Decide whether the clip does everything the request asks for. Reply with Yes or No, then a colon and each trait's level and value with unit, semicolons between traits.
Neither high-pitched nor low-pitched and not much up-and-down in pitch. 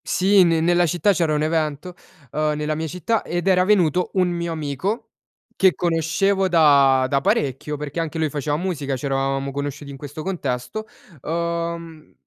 No: medium, 160 Hz; average, 3.5 semitones